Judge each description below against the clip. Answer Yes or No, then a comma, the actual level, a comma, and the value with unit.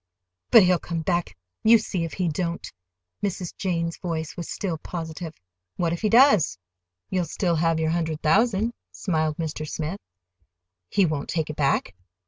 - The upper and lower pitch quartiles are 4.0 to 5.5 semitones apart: No, average, 2.8 semitones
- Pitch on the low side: No, medium, 170 Hz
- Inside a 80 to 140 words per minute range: No, average, 155 wpm